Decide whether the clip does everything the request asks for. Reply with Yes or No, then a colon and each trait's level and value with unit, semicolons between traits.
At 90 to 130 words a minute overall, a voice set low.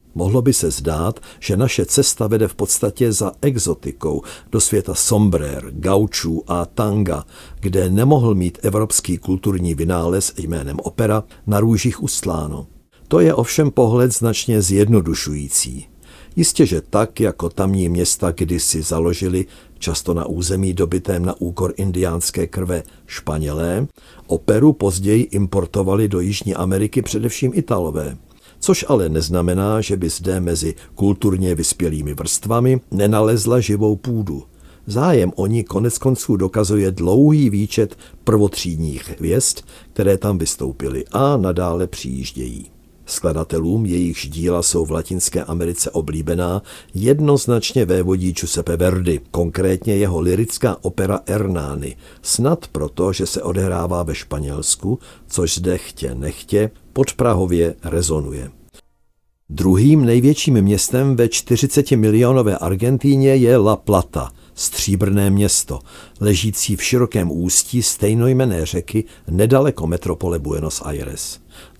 Yes: average, 120 wpm; very low, 95 Hz